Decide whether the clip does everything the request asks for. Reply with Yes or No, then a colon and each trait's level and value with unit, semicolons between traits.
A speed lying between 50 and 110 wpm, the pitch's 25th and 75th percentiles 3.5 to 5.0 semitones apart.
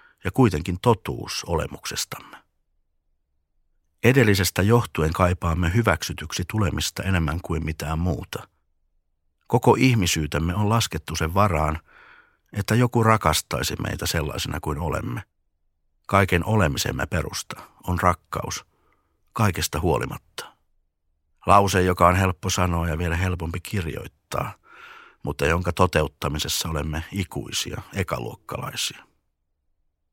Yes: slow, 95 wpm; average, 3.9 semitones